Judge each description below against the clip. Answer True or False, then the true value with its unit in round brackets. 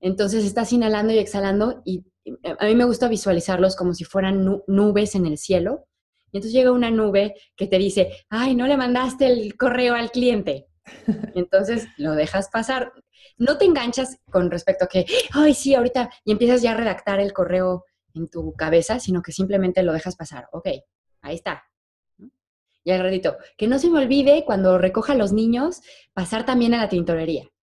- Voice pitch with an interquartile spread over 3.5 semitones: True (5.0 semitones)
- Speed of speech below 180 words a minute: False (185 wpm)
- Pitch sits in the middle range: False (210 Hz)